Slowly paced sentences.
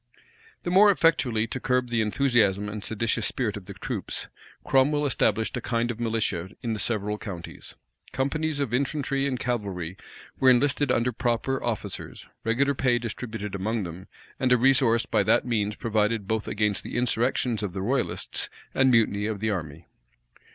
No: average, 165 wpm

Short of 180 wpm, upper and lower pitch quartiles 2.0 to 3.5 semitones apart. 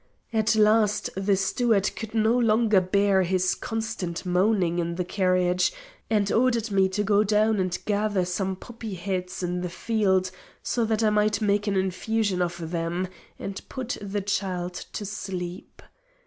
Yes: average, 160 wpm; average, 2.8 semitones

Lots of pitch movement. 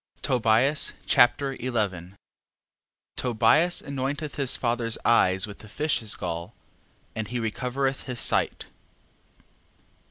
No: average, 3.9 semitones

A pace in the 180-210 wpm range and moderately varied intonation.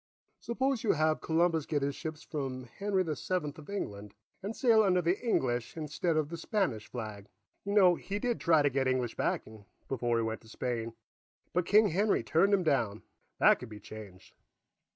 No: average, 190 wpm; wide, 7.7 semitones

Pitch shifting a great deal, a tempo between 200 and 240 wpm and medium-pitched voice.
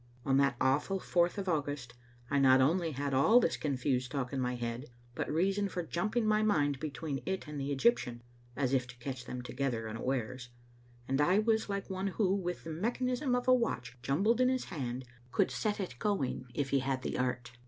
Yes: wide, 7.1 semitones; fast, 205 wpm; medium, 145 Hz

